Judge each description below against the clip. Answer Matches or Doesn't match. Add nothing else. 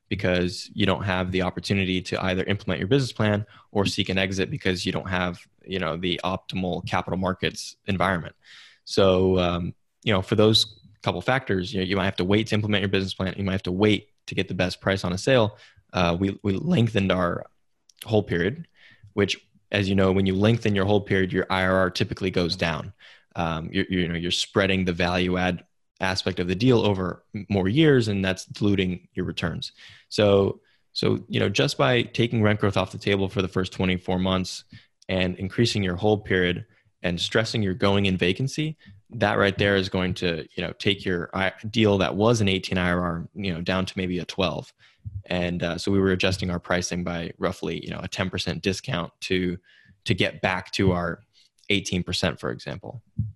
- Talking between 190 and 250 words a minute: Matches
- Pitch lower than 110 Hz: Matches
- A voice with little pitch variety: Matches